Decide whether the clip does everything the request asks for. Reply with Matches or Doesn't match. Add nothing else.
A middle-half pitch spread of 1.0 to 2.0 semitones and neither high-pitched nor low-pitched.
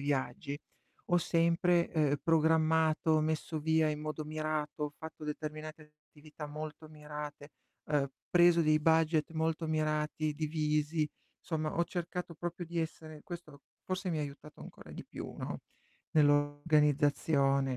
Matches